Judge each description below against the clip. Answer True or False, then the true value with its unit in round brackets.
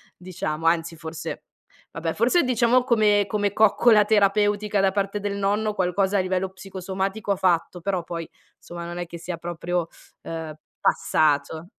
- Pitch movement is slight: False (3.2 semitones)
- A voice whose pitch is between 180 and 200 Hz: True (190 Hz)